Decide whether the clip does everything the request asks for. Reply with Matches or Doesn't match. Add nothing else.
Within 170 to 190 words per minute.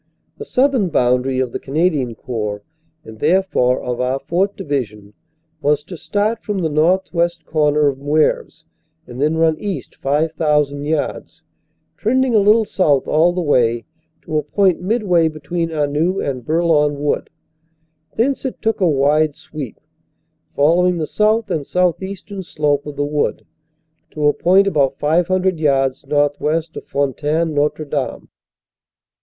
Doesn't match